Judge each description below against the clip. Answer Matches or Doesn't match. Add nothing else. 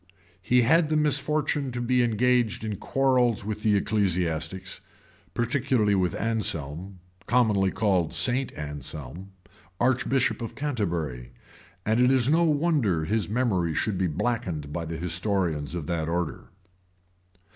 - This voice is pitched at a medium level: Doesn't match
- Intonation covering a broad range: Matches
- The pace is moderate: Doesn't match